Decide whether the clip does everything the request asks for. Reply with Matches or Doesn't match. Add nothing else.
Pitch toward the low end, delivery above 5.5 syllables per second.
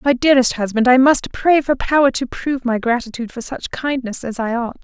Doesn't match